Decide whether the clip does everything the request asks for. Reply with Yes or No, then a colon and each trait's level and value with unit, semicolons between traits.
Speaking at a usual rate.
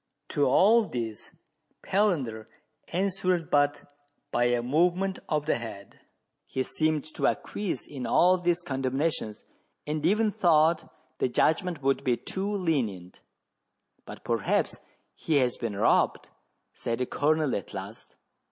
No: slow, 130 wpm